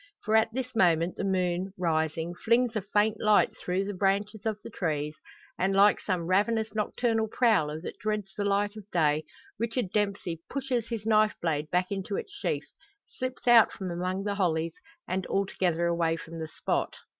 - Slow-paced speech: No, average, 180 wpm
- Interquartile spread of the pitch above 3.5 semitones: Yes, average, 3.9 semitones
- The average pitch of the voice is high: Yes, high, 195 Hz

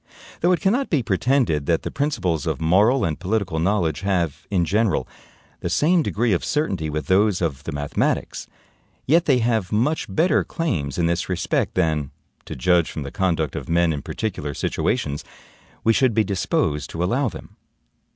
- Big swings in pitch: Yes, wide, 6.9 semitones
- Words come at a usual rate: Yes, average, 175 wpm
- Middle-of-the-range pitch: No, very low, 95 Hz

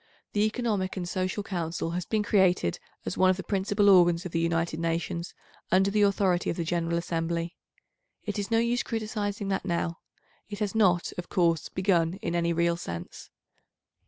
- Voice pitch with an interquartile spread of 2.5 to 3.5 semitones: Yes, average, 3.2 semitones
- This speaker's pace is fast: No, average, 180 wpm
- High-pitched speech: No, medium, 180 Hz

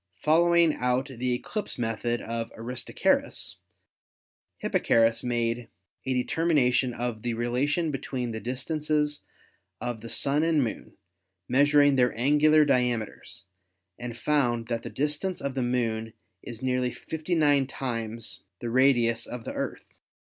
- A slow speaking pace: Yes, slow, 125 wpm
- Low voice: Yes, low, 125 Hz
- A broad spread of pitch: No, average, 3.8 semitones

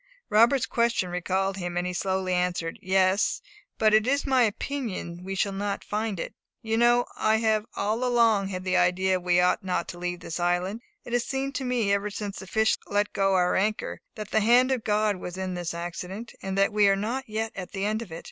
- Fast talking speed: Yes, fast, 225 wpm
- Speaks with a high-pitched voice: Yes, high, 200 Hz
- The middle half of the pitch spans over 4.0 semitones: No, average, 3.4 semitones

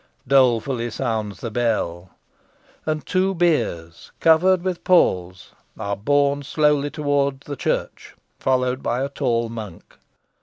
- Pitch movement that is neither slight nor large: Yes, average, 4.7 semitones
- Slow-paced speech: Yes, slow, 120 wpm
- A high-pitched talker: No, low, 135 Hz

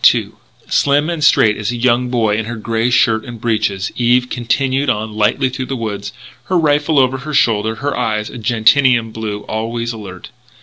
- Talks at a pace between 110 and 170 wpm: No, average, 185 wpm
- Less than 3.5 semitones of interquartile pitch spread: Yes, average, 3.0 semitones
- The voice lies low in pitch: Yes, low, 120 Hz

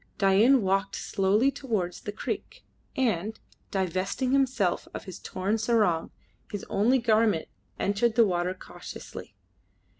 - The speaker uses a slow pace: Yes, slow, 120 wpm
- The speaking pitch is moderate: No, high, 205 Hz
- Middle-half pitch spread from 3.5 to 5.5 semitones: Yes, average, 3.8 semitones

